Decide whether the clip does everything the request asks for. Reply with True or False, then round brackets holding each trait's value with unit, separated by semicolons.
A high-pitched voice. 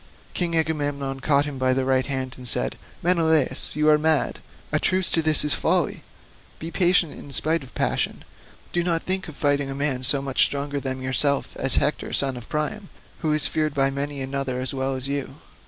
False (140 Hz)